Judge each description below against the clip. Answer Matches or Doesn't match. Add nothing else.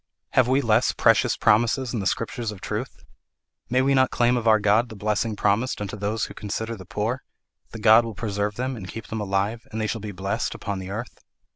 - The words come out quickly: Matches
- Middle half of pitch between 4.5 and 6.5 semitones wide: Doesn't match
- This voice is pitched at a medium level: Doesn't match